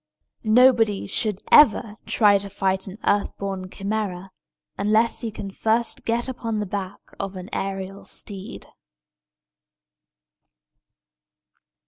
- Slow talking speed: Yes, slow, 110 wpm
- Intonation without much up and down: Yes, narrow, 2.3 semitones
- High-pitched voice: Yes, high, 200 Hz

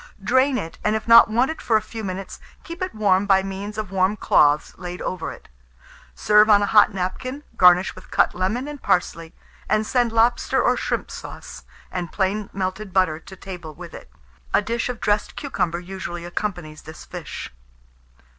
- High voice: Yes, high, 195 Hz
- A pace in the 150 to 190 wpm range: Yes, average, 180 wpm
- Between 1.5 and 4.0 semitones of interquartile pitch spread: Yes, average, 3.5 semitones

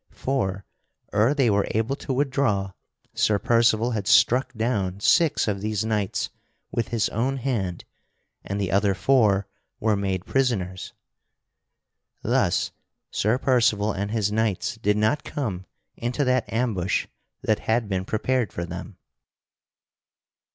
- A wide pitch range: No, average, 3.9 semitones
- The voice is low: Yes, low, 110 Hz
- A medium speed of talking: No, slow, 130 wpm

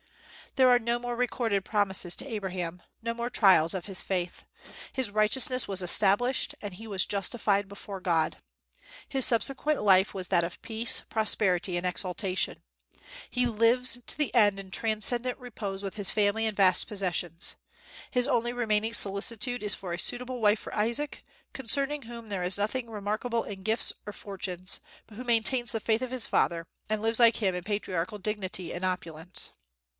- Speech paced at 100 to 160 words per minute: No, average, 170 wpm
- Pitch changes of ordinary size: Yes, average, 3.8 semitones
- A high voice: Yes, high, 210 Hz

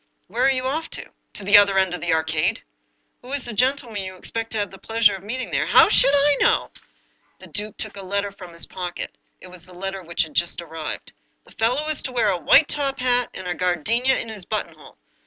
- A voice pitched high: Yes, high, 205 Hz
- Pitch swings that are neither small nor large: No, wide, 5.7 semitones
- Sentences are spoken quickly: Yes, fast, 275 wpm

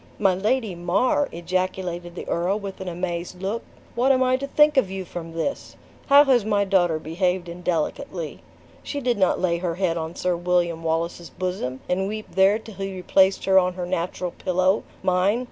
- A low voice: No, medium, 185 Hz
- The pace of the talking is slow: No, average, 185 wpm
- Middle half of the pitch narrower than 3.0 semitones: Yes, narrow, 2.6 semitones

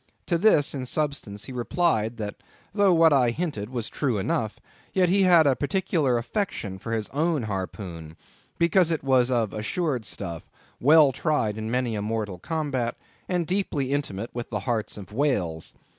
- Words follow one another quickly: No, average, 170 wpm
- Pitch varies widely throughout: Yes, wide, 6.7 semitones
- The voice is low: Yes, low, 125 Hz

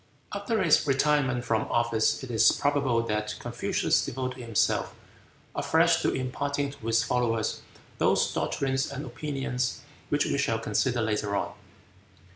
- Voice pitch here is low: Yes, low, 125 Hz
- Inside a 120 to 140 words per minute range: Yes, slow, 135 wpm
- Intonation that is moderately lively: Yes, average, 3.5 semitones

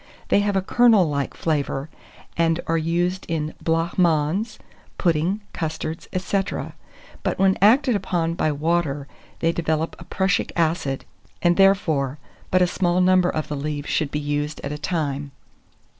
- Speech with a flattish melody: No, average, 3.5 semitones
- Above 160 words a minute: No, average, 150 wpm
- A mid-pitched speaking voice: Yes, medium, 165 Hz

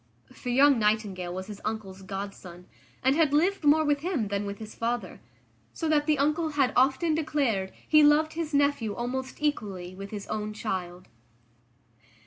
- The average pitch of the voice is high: Yes, high, 245 Hz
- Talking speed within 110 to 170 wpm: Yes, average, 165 wpm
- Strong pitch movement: Yes, wide, 6.7 semitones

